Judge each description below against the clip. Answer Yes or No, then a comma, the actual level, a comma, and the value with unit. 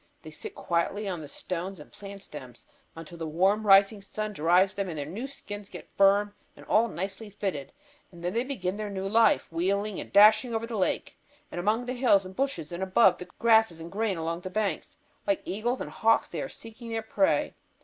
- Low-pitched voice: No, high, 200 Hz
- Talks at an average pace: No, fast, 210 wpm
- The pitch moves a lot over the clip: No, average, 3.7 semitones